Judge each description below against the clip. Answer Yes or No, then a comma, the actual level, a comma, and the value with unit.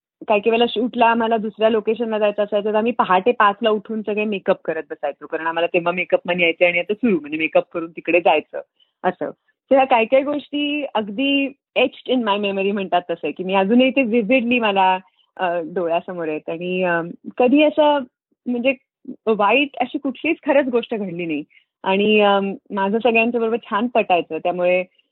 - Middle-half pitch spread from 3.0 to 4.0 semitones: No, wide, 5.5 semitones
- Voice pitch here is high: Yes, high, 215 Hz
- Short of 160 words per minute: No, fast, 165 wpm